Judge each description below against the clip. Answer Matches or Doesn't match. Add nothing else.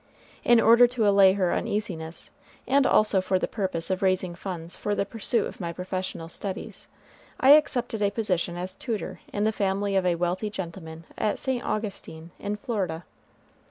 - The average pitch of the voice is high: Matches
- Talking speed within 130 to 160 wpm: Doesn't match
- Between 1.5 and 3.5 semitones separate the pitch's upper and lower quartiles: Matches